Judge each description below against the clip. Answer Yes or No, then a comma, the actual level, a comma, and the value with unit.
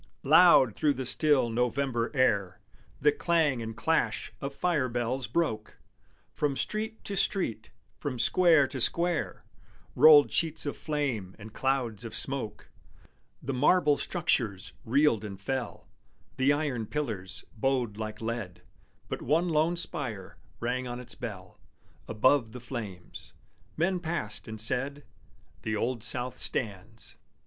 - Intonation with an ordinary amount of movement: Yes, average, 5.0 semitones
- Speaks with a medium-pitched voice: No, low, 125 Hz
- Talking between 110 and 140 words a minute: Yes, slow, 135 wpm